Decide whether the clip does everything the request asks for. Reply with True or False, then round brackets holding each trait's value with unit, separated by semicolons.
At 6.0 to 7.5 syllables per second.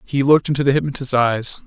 True (6.5 syllables/s)